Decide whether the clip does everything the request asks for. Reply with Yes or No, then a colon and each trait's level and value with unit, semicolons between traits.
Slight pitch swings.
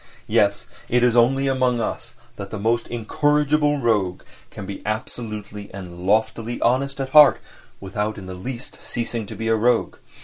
No: average, 4.0 semitones